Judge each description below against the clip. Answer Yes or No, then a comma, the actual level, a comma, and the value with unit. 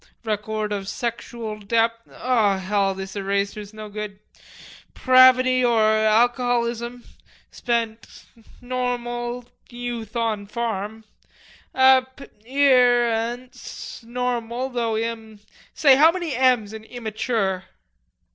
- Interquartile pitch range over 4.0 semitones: No, narrow, 2.4 semitones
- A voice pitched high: Yes, high, 235 Hz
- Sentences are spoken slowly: Yes, slow, 100 wpm